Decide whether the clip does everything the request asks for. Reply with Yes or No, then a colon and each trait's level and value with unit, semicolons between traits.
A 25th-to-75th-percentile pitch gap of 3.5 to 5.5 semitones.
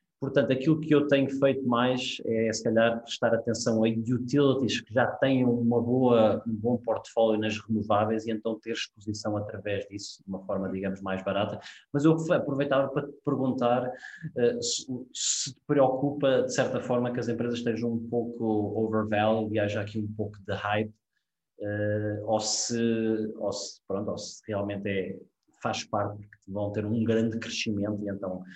No: average, 3.0 semitones